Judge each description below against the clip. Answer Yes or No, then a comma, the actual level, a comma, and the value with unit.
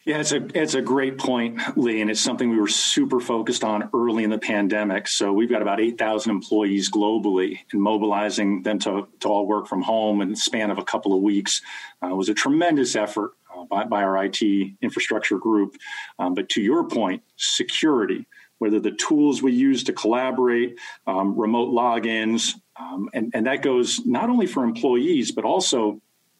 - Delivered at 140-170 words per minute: No, average, 190 wpm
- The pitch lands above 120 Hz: No, low, 115 Hz